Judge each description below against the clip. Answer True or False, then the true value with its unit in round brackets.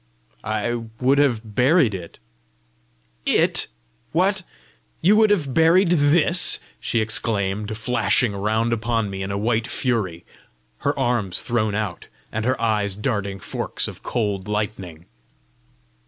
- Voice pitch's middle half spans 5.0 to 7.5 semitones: False (3.9 semitones)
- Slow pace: True (125 wpm)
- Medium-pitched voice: False (110 Hz)